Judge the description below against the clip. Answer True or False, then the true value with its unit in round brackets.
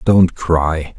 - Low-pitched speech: True (85 Hz)